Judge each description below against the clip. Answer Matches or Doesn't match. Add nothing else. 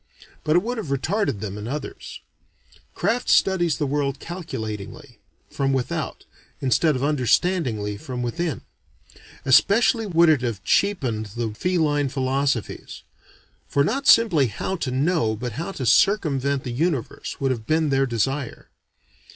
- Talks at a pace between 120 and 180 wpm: Matches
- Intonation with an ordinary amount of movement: Doesn't match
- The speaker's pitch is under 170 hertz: Matches